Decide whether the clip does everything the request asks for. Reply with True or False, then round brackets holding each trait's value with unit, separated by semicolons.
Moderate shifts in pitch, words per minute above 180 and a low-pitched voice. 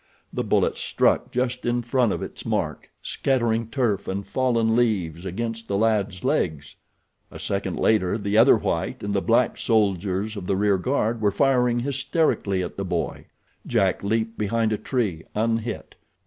False (3.3 semitones; 160 wpm; 110 Hz)